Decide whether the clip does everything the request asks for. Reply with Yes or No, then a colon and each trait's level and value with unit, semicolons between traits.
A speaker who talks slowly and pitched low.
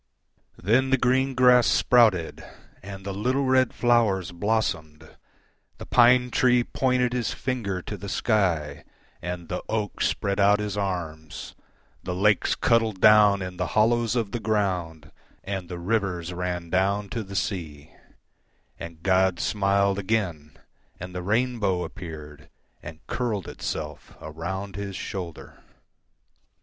Yes: slow, 115 wpm; low, 100 Hz